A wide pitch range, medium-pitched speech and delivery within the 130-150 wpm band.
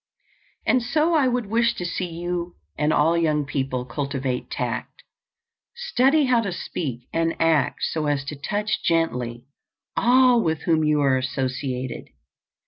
Yes: wide, 8.6 semitones; medium, 165 Hz; average, 145 wpm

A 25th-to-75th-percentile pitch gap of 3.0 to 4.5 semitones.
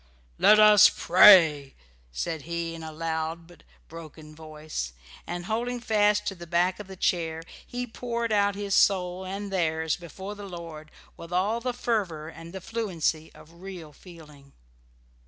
Yes: average, 4.1 semitones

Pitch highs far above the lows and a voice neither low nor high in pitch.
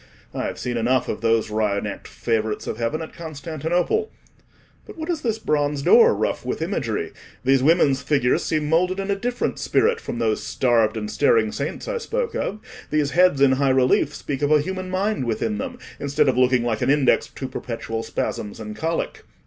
Yes: wide, 7.4 semitones; medium, 145 Hz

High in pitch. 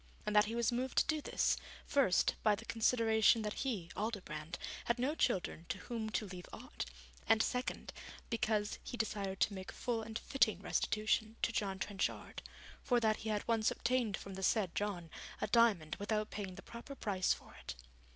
Yes: high, 215 Hz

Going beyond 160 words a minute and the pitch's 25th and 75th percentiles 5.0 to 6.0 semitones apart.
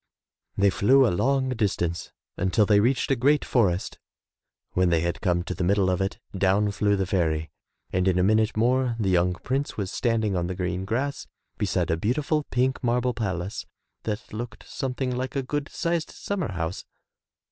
Yes: average, 180 wpm; wide, 5.6 semitones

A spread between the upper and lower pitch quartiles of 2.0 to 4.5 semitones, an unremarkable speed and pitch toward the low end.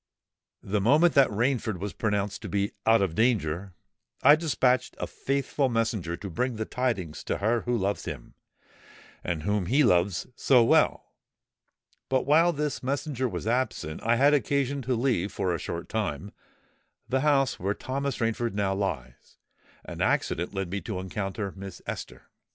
No: average, 5.2 semitones; average, 160 wpm; low, 110 Hz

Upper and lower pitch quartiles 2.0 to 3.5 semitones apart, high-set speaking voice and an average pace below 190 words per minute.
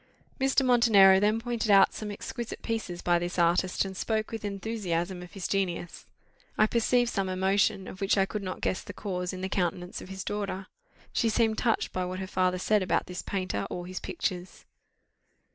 No: average, 2.9 semitones; high, 195 Hz; average, 195 wpm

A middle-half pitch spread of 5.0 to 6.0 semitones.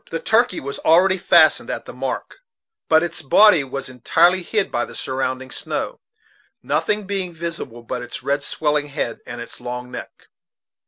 Yes: wide, 5.4 semitones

